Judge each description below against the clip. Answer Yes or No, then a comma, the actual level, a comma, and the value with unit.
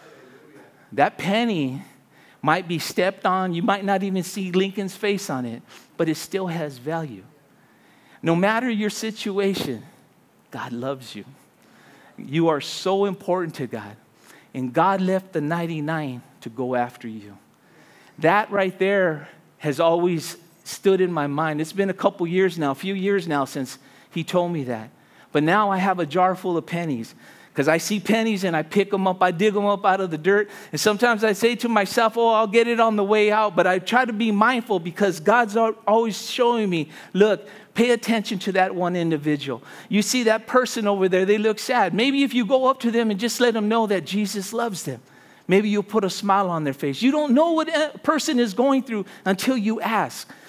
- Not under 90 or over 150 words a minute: No, average, 200 wpm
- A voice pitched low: No, high, 195 Hz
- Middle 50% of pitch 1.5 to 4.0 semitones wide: No, average, 5.0 semitones